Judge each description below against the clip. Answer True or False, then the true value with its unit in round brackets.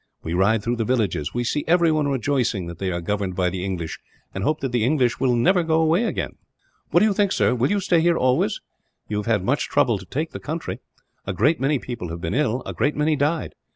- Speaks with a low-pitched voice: True (125 Hz)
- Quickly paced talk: True (245 wpm)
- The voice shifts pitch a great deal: True (7.4 semitones)